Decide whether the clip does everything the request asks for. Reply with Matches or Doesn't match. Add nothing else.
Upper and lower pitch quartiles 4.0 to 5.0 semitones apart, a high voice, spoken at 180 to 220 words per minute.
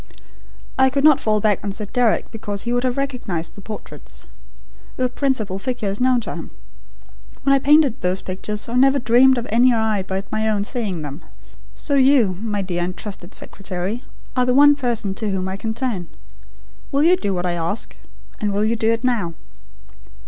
Matches